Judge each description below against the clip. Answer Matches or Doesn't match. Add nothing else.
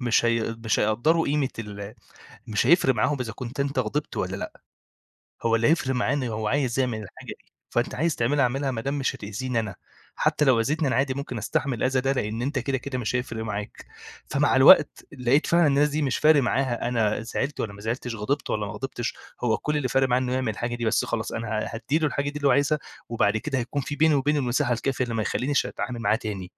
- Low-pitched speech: Matches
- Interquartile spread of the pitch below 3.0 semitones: Doesn't match